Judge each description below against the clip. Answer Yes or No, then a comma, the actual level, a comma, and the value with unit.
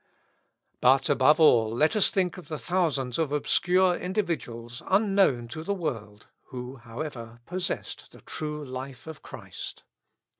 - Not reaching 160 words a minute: Yes, average, 140 wpm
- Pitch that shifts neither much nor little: No, wide, 6.3 semitones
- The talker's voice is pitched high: No, medium, 150 Hz